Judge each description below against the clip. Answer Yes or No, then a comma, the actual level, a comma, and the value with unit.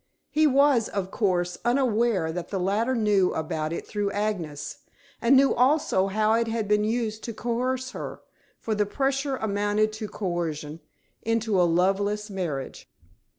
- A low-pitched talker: No, high, 210 Hz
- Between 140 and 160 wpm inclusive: Yes, average, 150 wpm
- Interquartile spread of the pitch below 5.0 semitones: Yes, average, 4.0 semitones